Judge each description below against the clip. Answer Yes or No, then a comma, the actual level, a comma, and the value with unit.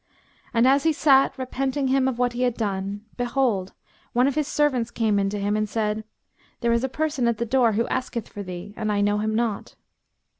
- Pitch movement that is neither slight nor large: Yes, average, 4.0 semitones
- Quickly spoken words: Yes, fast, 220 wpm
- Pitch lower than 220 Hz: No, high, 235 Hz